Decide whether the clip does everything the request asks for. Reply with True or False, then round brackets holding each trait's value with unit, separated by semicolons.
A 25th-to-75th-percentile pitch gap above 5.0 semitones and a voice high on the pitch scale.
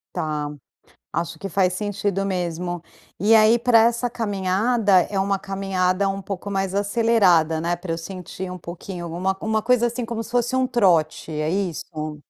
False (3.9 semitones; 195 Hz)